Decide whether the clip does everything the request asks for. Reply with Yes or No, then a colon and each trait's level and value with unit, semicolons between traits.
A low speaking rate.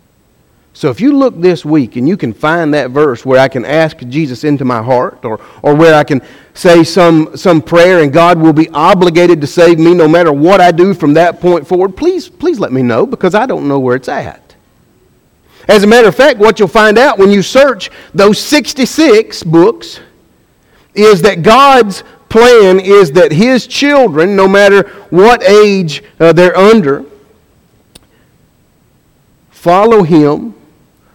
No: average, 175 wpm